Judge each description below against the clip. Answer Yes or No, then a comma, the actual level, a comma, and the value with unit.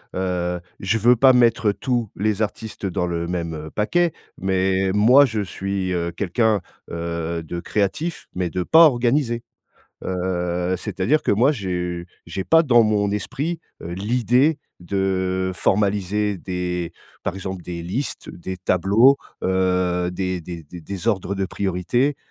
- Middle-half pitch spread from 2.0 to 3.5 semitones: No, average, 4.2 semitones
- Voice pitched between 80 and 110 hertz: Yes, very low, 95 Hz